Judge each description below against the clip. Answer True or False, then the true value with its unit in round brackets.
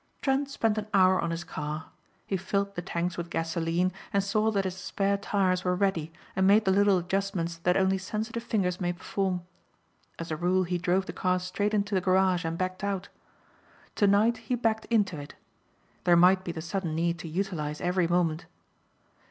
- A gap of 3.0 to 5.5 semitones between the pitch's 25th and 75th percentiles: False (2.5 semitones)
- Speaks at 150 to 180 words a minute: False (190 wpm)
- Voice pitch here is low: False (185 Hz)